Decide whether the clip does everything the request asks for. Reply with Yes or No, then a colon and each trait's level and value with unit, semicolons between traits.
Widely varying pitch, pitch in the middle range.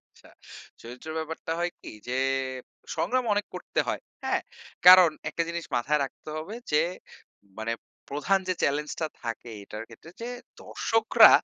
Yes: wide, 5.9 semitones; medium, 155 Hz